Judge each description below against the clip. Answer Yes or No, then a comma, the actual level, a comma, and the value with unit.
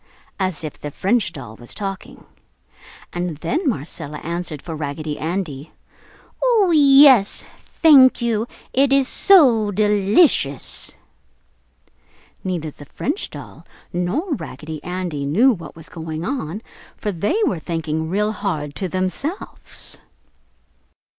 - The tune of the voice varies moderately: No, wide, 7.6 semitones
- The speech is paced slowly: Yes, slow, 120 wpm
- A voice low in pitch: No, medium, 185 Hz